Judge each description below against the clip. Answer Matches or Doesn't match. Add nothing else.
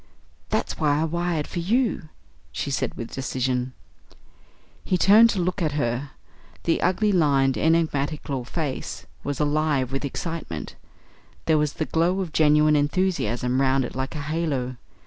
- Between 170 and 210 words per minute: Doesn't match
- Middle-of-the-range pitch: Matches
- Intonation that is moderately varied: Matches